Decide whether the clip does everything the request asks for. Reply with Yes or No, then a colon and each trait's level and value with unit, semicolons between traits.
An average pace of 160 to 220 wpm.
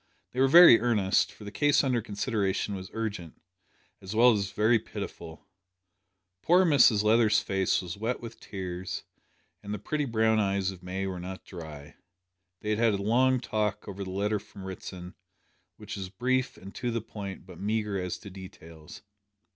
Yes: average, 175 wpm